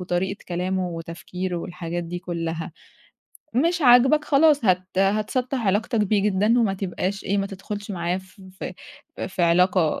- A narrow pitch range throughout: No, average, 3.3 semitones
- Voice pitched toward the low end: No, high, 190 Hz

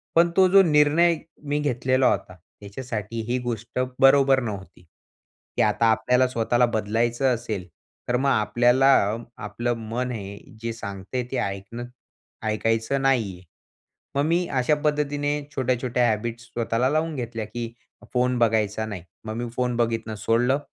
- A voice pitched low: Yes, low, 120 Hz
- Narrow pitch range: No, average, 3.3 semitones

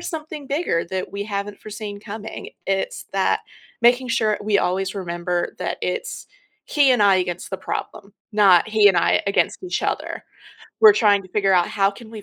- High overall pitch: Yes, high, 205 Hz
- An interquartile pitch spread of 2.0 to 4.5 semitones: Yes, narrow, 2.5 semitones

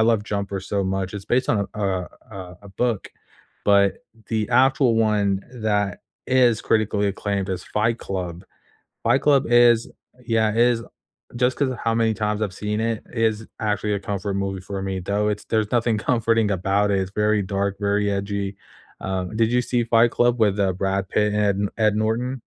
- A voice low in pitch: Yes, low, 105 Hz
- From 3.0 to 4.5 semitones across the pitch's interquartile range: No, narrow, 2.5 semitones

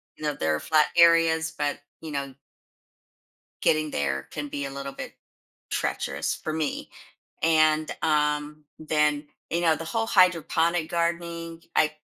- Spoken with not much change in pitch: Yes, narrow, 2.1 semitones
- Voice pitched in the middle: Yes, medium, 155 Hz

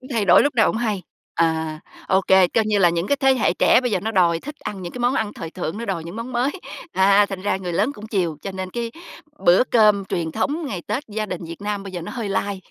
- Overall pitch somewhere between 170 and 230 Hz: Yes, high, 200 Hz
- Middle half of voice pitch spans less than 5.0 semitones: Yes, average, 4.2 semitones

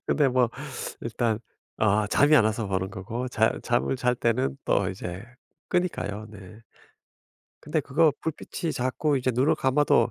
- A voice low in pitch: Yes, low, 120 Hz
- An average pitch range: Yes, average, 4.6 semitones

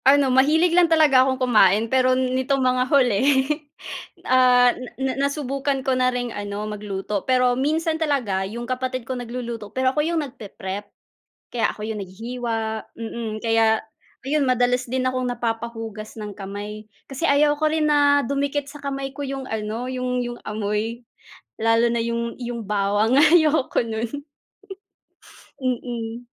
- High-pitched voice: Yes, very high, 250 Hz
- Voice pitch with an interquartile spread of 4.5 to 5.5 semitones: No, average, 3.3 semitones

